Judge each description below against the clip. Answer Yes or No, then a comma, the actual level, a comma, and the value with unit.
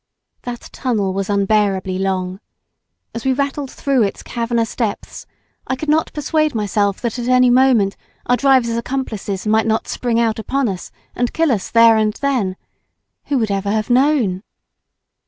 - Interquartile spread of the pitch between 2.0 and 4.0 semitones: No, average, 4.4 semitones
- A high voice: Yes, high, 230 Hz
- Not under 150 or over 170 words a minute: Yes, average, 160 wpm